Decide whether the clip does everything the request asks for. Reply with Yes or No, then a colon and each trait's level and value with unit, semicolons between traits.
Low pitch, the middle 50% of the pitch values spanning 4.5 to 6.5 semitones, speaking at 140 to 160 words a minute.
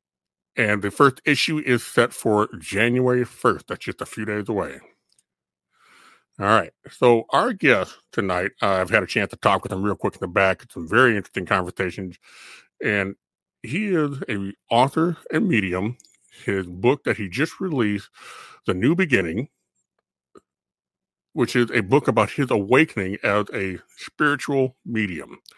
Yes: low, 110 Hz; average, 5.0 semitones; average, 155 wpm